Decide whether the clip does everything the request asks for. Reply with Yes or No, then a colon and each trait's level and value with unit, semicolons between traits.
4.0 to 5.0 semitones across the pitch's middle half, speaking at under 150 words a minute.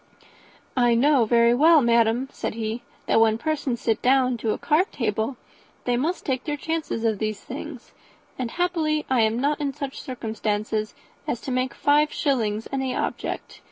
No: average, 4.4 semitones; average, 170 wpm